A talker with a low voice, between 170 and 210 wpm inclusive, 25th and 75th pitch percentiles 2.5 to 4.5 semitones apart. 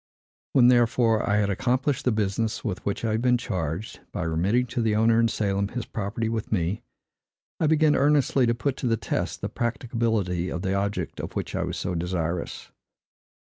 Yes: low, 110 Hz; average, 190 wpm; average, 3.8 semitones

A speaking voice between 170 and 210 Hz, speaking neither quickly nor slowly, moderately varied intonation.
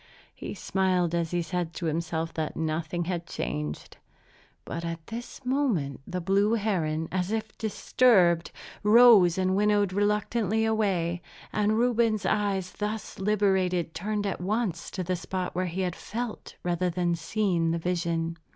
Yes: medium, 185 Hz; average, 150 wpm; average, 3.8 semitones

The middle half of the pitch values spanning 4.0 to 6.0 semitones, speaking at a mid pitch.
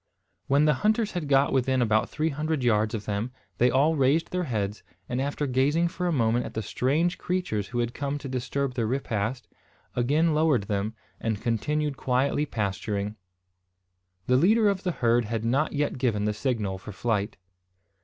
No: average, 5.2 semitones; low, 130 Hz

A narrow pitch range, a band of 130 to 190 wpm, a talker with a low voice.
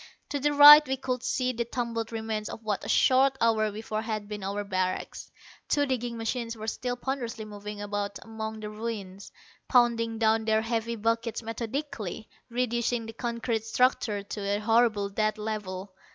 No: narrow, 2.2 semitones; average, 165 wpm; high, 225 Hz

